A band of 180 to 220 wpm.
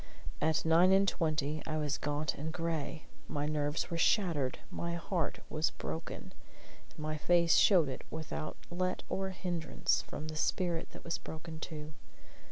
No: average, 160 wpm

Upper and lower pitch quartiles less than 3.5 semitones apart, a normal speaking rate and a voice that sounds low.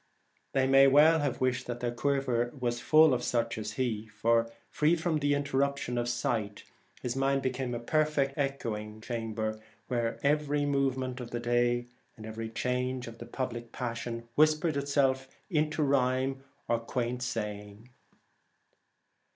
Yes: average, 3.1 semitones; average, 145 wpm; low, 125 Hz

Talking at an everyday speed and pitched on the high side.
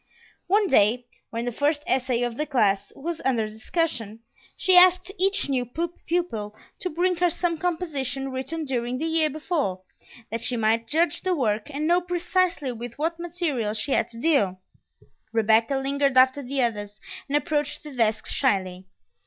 Yes: average, 165 wpm; very high, 275 Hz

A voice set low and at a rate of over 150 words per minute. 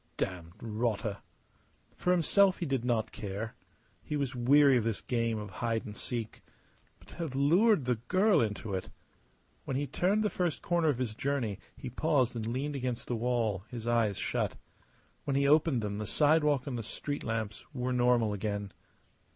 Yes: low, 125 Hz; average, 180 wpm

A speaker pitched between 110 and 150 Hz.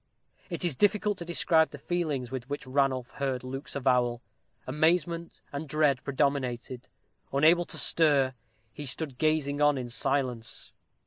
Yes: medium, 140 Hz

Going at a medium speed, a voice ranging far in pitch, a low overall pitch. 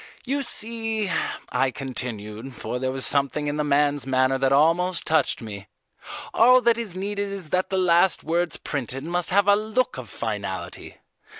No: average, 170 wpm; wide, 7.0 semitones; medium, 160 Hz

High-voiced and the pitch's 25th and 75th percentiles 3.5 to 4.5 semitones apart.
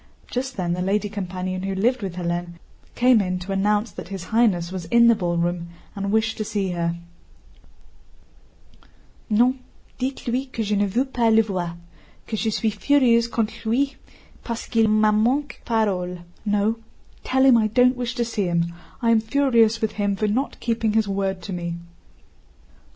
Yes: high, 215 Hz; average, 3.9 semitones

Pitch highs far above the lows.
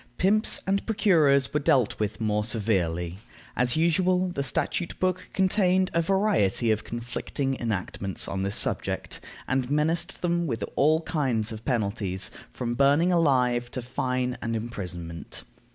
Yes: wide, 7.6 semitones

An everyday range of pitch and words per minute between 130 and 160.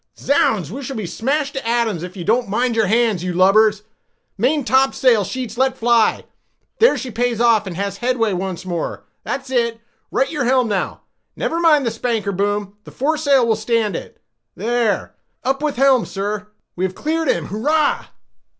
Yes: average, 4.5 semitones; average, 155 wpm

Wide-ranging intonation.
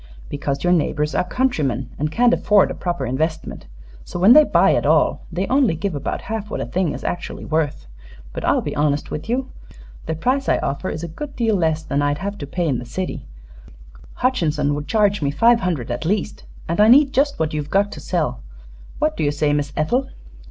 Yes: wide, 6.6 semitones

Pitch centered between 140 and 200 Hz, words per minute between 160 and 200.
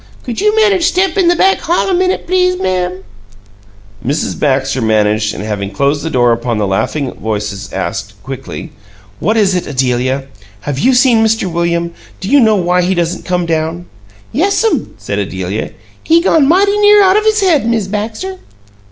Yes: medium, 185 Hz; average, 175 wpm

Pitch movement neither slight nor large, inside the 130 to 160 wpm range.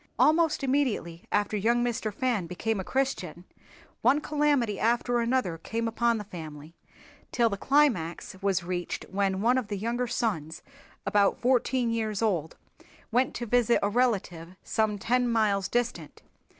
Yes: average, 4.3 semitones; average, 150 wpm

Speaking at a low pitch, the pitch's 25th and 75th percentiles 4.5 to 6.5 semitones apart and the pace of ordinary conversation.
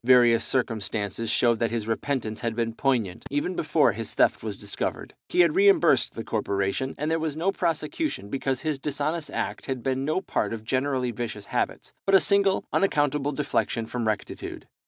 Yes: low, 130 Hz; average, 5.2 semitones; average, 180 wpm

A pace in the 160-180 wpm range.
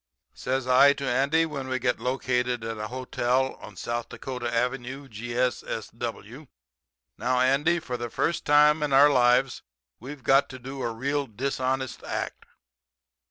No: average, 150 wpm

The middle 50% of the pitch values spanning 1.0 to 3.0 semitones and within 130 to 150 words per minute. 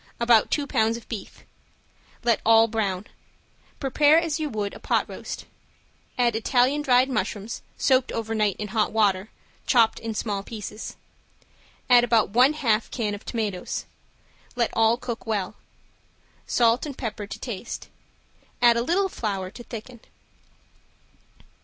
Yes: average, 2.7 semitones; average, 140 wpm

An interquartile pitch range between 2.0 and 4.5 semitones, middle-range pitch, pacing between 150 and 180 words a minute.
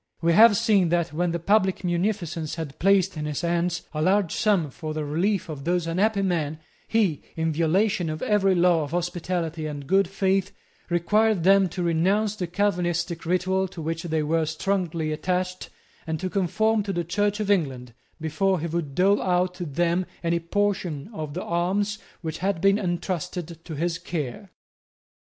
Yes: average, 3.1 semitones; medium, 175 Hz; average, 175 wpm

